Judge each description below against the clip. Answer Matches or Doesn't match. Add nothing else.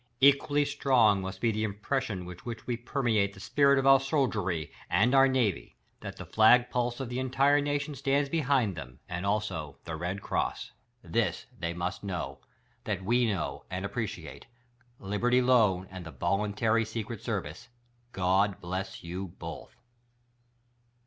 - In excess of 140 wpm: Matches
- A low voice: Matches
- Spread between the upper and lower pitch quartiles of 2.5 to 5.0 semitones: Doesn't match